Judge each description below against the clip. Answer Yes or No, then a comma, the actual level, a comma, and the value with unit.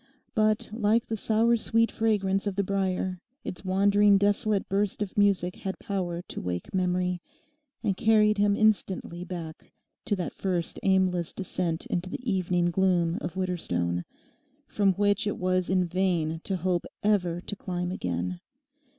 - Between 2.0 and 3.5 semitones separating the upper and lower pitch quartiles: Yes, narrow, 2.5 semitones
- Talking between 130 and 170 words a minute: Yes, average, 150 wpm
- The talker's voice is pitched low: No, high, 190 Hz